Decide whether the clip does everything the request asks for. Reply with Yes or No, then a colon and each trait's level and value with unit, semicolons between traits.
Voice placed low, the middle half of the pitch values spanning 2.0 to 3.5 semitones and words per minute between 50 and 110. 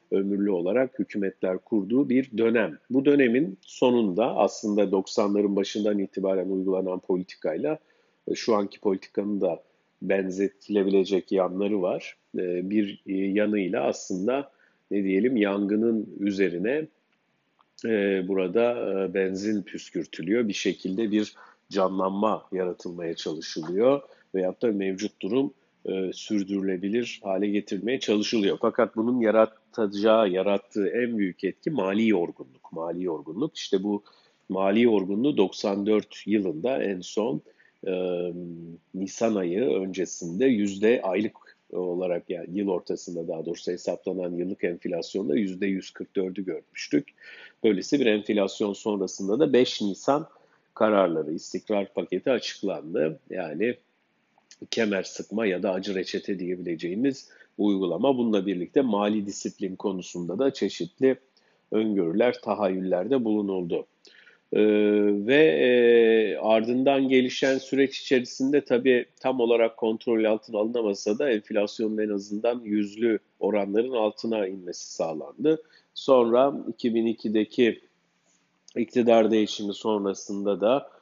Yes: low, 105 Hz; average, 3.0 semitones; average, 105 wpm